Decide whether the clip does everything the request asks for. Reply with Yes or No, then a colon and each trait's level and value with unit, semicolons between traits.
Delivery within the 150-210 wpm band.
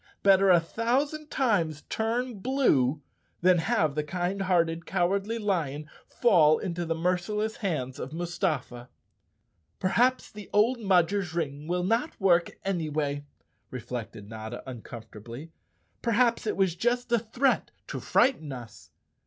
No: slow, 135 wpm